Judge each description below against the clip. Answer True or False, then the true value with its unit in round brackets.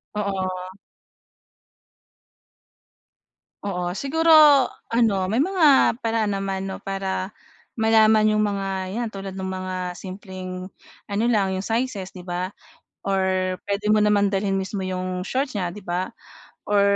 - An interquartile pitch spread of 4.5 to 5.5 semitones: False (2.6 semitones)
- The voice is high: True (195 Hz)